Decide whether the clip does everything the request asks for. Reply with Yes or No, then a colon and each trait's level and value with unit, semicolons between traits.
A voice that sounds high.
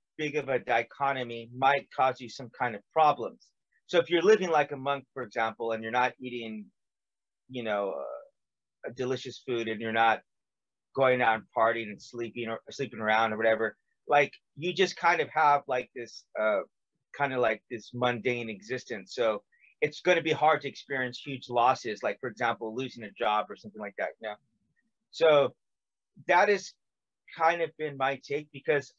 No: low, 125 Hz